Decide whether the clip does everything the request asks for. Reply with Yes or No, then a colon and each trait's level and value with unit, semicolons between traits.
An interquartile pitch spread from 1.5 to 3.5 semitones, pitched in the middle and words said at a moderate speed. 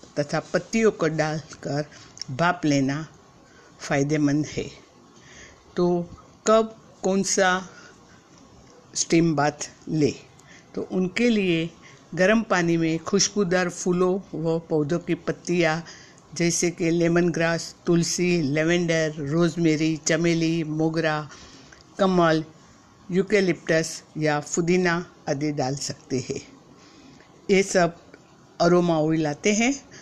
No: narrow, 2.5 semitones; medium, 165 Hz; slow, 100 wpm